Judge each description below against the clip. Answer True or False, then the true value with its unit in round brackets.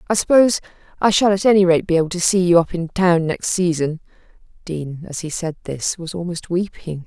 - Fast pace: True (220 wpm)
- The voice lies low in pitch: False (175 Hz)